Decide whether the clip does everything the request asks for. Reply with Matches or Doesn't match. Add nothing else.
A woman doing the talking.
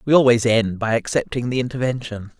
Doesn't match